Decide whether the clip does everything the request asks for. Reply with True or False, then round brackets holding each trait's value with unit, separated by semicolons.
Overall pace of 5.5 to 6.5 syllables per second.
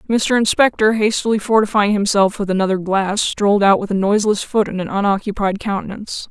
True (5.9 syllables/s)